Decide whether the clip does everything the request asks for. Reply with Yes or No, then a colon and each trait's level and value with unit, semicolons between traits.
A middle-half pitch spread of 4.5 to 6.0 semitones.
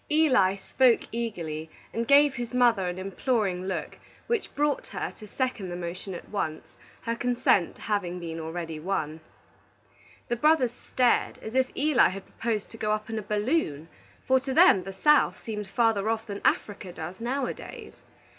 Yes: average, 5.2 semitones